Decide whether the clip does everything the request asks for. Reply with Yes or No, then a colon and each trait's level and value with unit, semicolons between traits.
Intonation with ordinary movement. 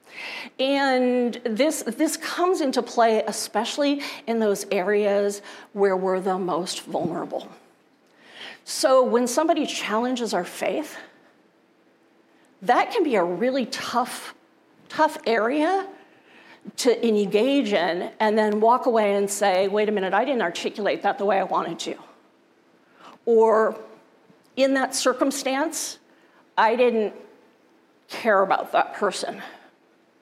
Yes: average, 5.0 semitones